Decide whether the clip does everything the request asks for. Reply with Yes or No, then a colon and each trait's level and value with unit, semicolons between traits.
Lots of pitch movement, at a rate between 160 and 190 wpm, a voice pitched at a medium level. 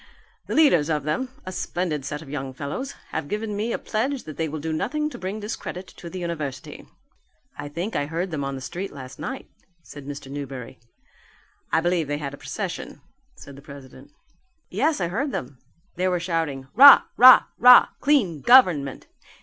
Yes: wide, 6.6 semitones; average, 185 wpm; medium, 165 Hz